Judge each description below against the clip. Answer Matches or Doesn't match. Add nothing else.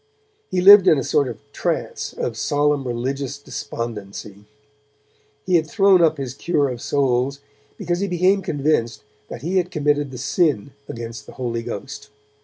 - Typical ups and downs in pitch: Doesn't match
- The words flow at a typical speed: Matches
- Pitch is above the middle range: Doesn't match